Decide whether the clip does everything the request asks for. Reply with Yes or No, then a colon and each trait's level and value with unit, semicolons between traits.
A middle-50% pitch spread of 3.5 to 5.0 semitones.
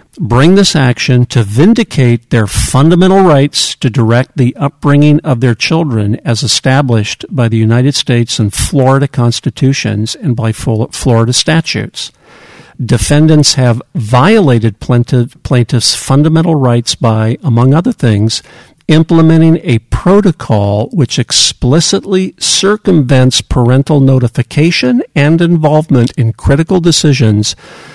Yes: average, 4.7 semitones